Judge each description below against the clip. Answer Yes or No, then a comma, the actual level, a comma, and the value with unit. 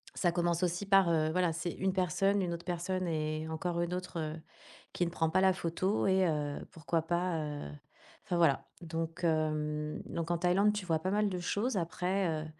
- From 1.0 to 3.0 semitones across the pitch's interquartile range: Yes, narrow, 2.5 semitones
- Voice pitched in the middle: Yes, medium, 175 Hz